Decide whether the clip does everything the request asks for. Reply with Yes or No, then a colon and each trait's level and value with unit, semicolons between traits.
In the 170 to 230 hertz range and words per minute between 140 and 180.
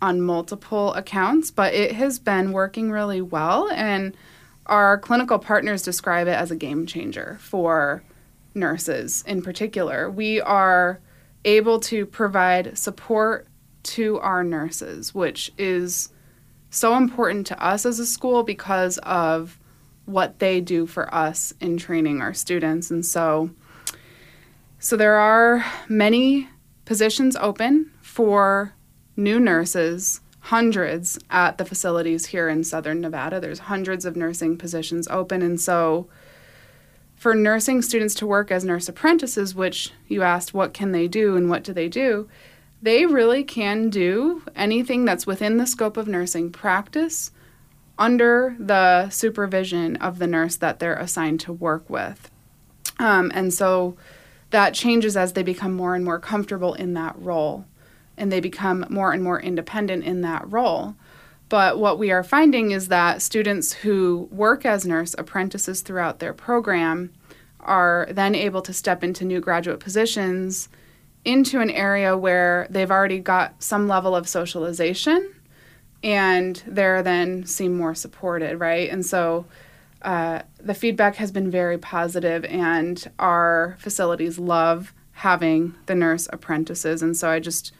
Yes: medium, 185 Hz; average, 145 wpm